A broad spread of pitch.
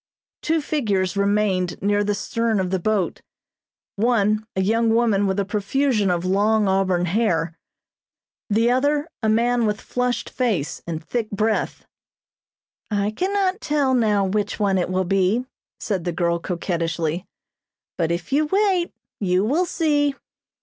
No: average, 4.5 semitones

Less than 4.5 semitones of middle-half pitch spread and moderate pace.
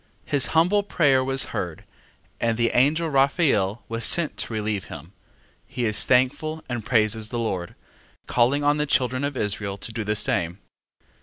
No: average, 5.0 semitones; average, 165 wpm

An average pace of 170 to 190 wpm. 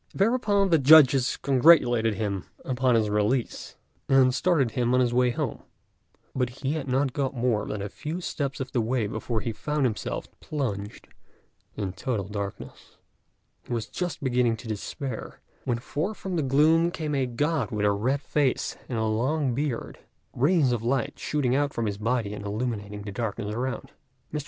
Yes: average, 175 wpm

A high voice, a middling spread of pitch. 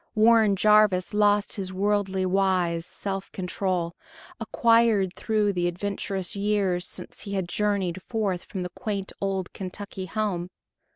No: high, 195 Hz; narrow, 2.2 semitones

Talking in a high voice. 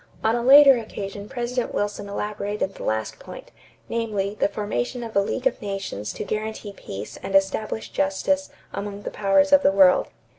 Yes: high, 205 Hz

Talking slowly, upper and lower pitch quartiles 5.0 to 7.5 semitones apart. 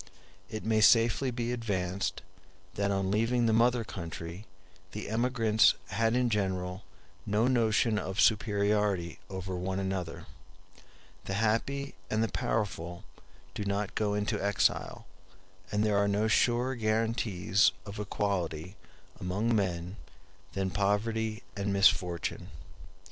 No: slow, 120 wpm; average, 2.8 semitones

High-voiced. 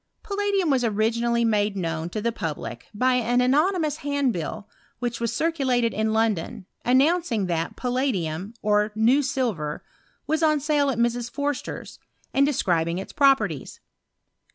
Yes: high, 235 Hz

